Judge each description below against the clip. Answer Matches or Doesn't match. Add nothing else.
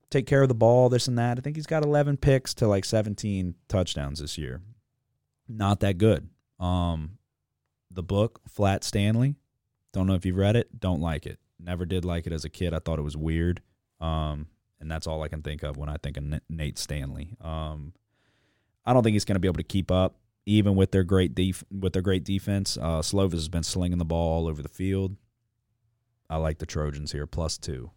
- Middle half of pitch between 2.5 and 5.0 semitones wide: Doesn't match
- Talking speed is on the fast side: Matches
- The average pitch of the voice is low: Matches